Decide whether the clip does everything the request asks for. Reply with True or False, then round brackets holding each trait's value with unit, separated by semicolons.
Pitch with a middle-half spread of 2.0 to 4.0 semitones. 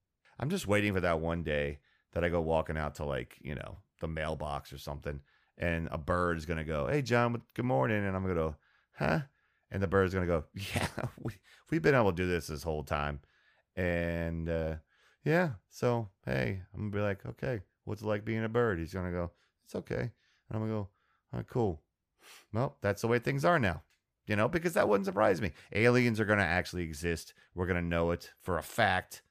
False (4.8 semitones)